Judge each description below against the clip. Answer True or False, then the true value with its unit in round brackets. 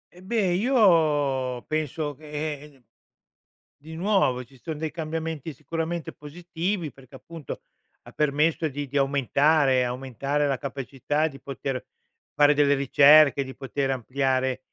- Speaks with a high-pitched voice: False (145 Hz)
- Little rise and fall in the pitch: False (3.0 semitones)